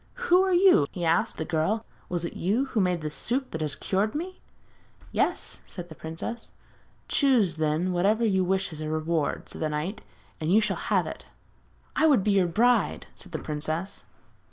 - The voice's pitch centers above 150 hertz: Yes, medium, 185 Hz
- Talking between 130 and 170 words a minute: No, average, 190 wpm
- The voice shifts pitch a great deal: Yes, wide, 6.0 semitones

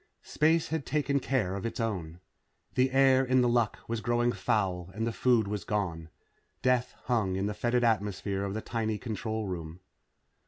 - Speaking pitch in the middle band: No, low, 110 Hz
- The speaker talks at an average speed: Yes, average, 180 wpm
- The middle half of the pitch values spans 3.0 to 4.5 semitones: Yes, average, 4.0 semitones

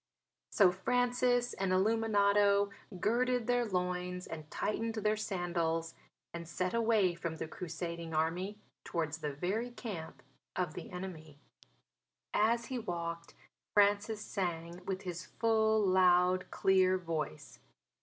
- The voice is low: No, medium, 185 Hz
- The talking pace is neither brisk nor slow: No, slow, 120 wpm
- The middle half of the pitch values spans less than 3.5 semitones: No, average, 4.3 semitones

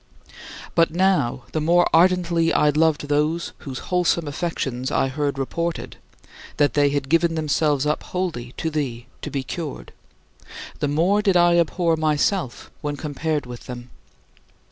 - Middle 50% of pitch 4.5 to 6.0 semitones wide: No, average, 3.1 semitones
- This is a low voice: No, medium, 155 Hz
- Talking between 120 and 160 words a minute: Yes, average, 150 wpm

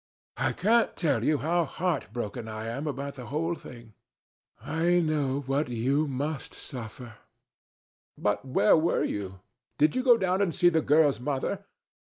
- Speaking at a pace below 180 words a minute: Yes, average, 160 wpm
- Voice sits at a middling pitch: Yes, medium, 145 Hz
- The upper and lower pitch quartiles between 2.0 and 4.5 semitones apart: No, average, 5.2 semitones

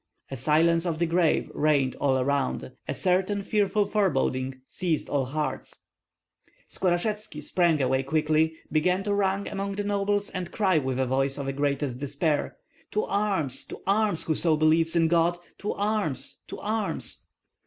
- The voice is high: No, medium, 165 Hz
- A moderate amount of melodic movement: No, wide, 5.7 semitones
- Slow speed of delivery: No, average, 155 wpm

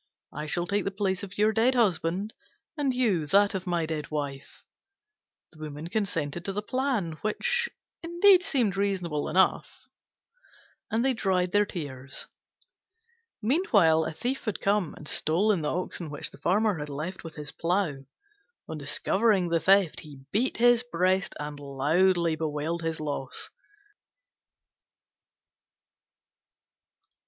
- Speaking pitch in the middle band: Yes, medium, 180 Hz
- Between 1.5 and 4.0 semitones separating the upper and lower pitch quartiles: No, average, 5.2 semitones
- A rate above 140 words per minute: No, slow, 135 wpm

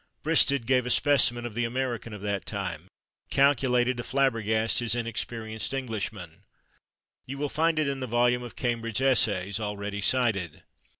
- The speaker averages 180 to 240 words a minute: No, average, 155 wpm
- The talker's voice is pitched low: Yes, low, 120 Hz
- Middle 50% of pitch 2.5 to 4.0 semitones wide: Yes, average, 3.7 semitones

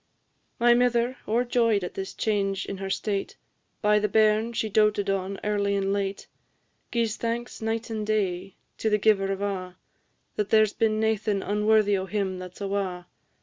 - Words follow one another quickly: No, average, 170 wpm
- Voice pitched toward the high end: Yes, high, 210 Hz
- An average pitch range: No, narrow, 2.1 semitones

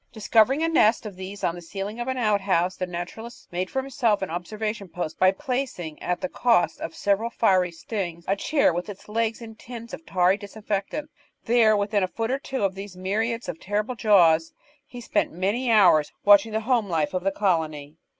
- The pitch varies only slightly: No, average, 4.0 semitones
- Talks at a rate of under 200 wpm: No, fast, 205 wpm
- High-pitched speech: Yes, high, 205 Hz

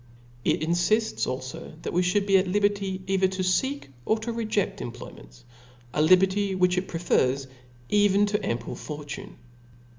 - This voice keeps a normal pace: Yes, average, 150 wpm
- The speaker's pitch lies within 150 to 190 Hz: Yes, medium, 185 Hz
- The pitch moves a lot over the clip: No, average, 4.3 semitones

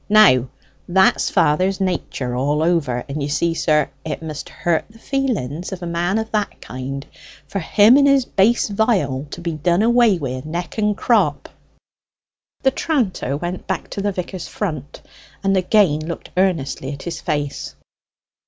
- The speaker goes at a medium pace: Yes, average, 160 wpm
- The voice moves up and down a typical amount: No, wide, 5.9 semitones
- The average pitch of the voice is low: No, medium, 175 Hz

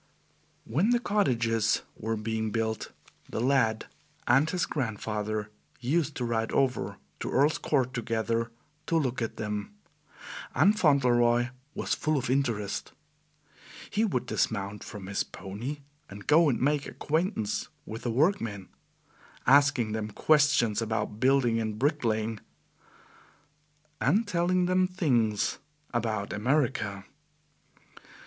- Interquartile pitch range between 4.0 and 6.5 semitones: Yes, average, 5.1 semitones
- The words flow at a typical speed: No, slow, 120 wpm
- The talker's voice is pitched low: Yes, low, 120 Hz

